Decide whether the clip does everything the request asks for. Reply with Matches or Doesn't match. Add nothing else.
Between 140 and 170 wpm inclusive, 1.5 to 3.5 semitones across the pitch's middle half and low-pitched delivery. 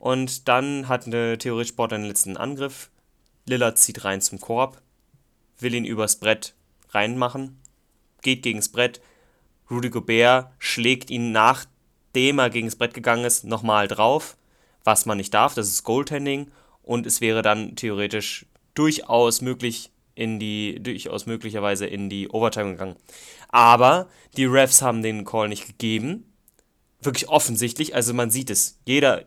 Matches